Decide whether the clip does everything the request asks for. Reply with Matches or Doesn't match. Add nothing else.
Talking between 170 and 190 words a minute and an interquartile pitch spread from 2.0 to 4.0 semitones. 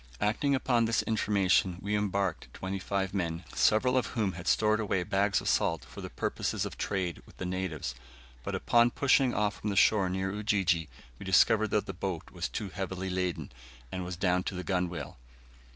Matches